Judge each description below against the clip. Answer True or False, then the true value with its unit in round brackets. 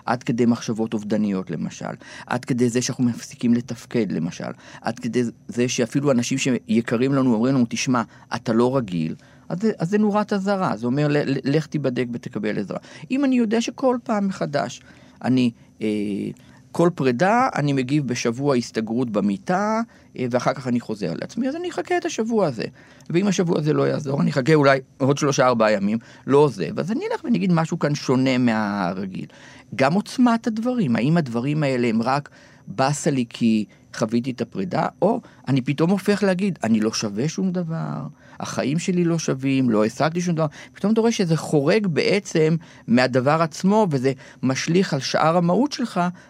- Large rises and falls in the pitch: True (7.2 semitones)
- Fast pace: True (170 wpm)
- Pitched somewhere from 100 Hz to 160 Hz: True (140 Hz)